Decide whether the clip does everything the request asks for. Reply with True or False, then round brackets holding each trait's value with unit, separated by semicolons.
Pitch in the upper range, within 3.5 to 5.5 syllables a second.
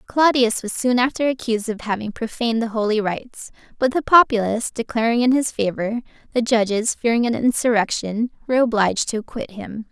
False (230 Hz; 5.8 syllables/s)